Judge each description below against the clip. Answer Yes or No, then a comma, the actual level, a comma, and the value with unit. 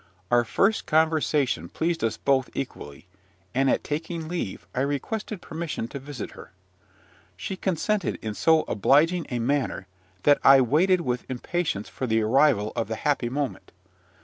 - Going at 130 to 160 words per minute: Yes, average, 150 wpm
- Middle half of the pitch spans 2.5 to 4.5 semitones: No, average, 5.2 semitones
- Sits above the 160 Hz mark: No, medium, 140 Hz